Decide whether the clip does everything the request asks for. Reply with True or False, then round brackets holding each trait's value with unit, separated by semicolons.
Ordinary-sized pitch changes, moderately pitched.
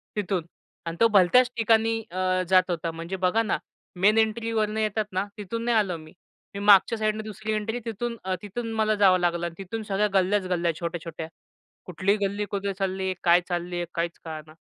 False (3.4 semitones; 195 Hz)